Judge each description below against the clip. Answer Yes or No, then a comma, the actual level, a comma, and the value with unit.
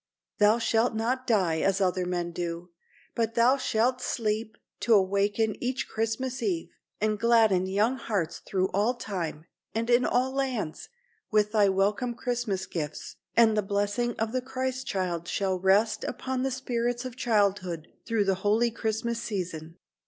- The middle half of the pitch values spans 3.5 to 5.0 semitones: Yes, average, 4.0 semitones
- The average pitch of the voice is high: Yes, high, 220 Hz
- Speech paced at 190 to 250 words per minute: No, average, 155 wpm